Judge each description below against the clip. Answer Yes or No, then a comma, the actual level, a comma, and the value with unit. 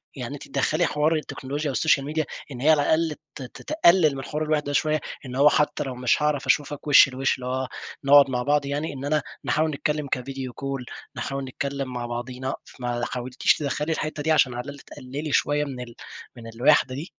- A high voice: No, medium, 140 Hz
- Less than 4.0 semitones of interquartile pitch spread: Yes, average, 2.7 semitones